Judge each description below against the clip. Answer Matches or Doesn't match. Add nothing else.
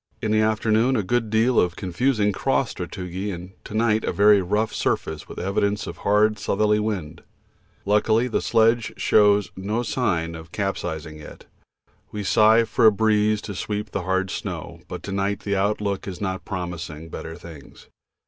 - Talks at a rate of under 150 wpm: Doesn't match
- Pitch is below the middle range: Matches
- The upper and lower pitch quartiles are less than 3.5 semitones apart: Matches